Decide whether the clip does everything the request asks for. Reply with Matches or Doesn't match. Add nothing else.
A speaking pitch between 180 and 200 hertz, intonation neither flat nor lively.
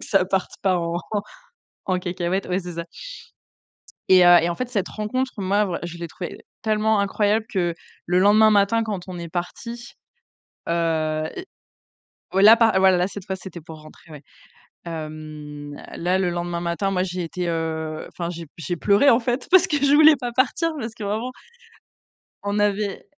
Matches